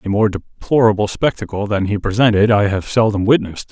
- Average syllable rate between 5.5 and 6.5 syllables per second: Yes, 5.8 syllables/s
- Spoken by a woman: No, male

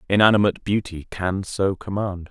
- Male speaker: Yes, male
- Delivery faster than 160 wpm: No, slow, 130 wpm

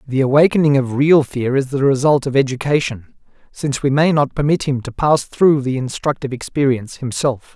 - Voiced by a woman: No, male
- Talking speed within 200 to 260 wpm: No, average, 185 wpm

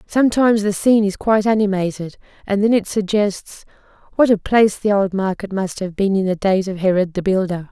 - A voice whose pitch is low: No, high, 200 Hz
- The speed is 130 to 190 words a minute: No, average, 200 wpm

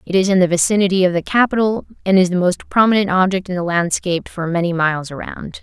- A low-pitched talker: No, medium, 185 Hz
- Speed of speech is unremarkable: No, fast, 225 wpm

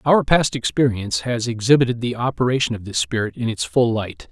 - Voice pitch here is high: No, low, 120 Hz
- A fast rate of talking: No, average, 195 wpm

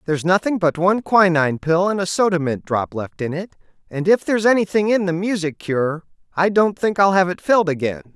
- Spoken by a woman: No, male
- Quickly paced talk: Yes, fast, 220 wpm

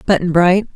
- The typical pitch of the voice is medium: Yes, medium, 175 Hz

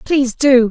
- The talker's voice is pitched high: Yes, very high, 255 Hz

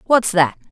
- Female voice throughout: Yes, female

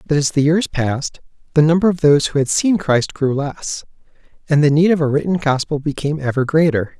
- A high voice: No, medium, 150 Hz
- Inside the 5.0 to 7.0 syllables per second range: Yes, 5.8 syllables/s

